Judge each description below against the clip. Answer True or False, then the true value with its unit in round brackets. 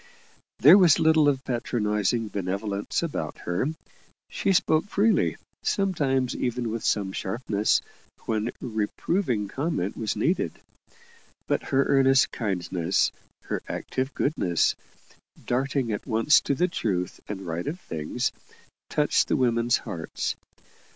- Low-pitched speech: True (120 Hz)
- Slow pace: True (120 wpm)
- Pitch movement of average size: False (5.7 semitones)